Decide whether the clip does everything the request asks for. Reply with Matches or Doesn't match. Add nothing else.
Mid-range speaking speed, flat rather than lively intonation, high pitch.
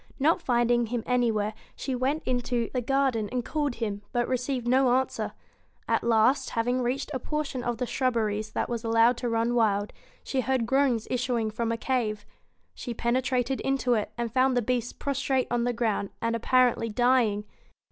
Matches